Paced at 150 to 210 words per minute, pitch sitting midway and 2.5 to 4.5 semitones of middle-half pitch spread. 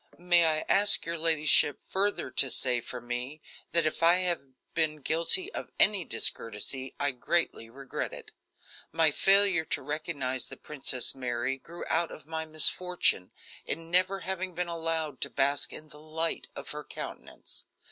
Yes: average, 160 wpm; medium, 155 Hz; average, 4.2 semitones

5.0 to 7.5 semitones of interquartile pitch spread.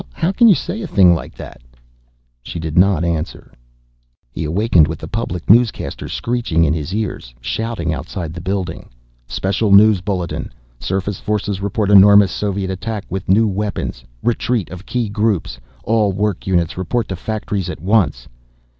No: average, 3.8 semitones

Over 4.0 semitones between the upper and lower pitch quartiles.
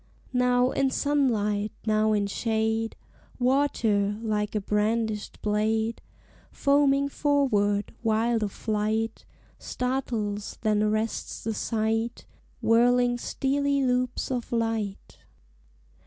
No: average, 2.9 semitones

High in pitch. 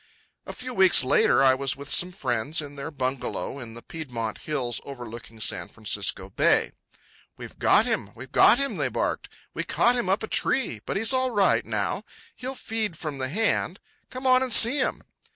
No: medium, 155 Hz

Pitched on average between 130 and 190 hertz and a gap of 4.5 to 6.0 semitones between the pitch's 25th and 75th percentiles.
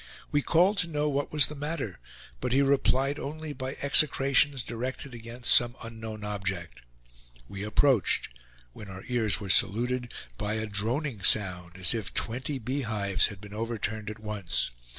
No: low, 115 Hz; average, 4.9 semitones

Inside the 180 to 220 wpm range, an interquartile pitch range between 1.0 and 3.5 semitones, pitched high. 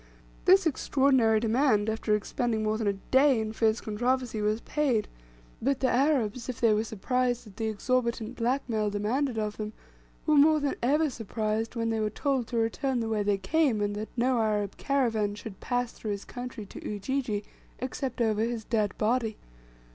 Yes: average, 185 wpm; average, 3.2 semitones; high, 230 Hz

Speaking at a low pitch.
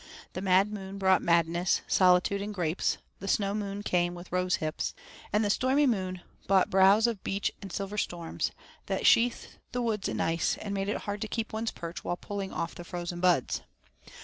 No: high, 195 Hz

